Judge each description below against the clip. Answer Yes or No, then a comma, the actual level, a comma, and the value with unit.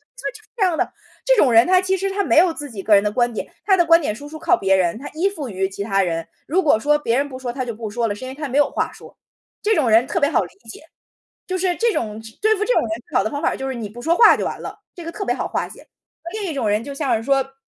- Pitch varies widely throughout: Yes, wide, 7.8 semitones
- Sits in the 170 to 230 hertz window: No, very high, 275 Hz